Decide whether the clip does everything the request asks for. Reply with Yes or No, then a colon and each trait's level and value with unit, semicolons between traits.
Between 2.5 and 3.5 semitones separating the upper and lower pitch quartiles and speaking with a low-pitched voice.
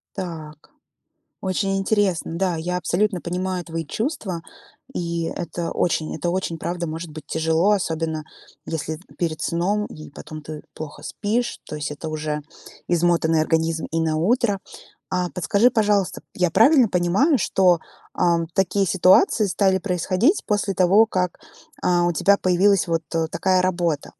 No: average, 3.1 semitones; medium, 175 Hz